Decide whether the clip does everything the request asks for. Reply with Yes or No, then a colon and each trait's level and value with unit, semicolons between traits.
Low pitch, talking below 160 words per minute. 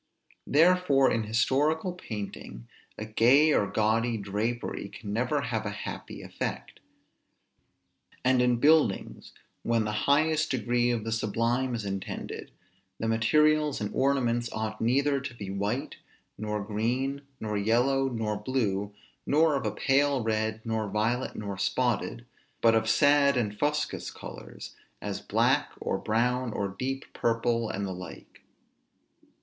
Yes: low, 115 Hz; slow, 135 wpm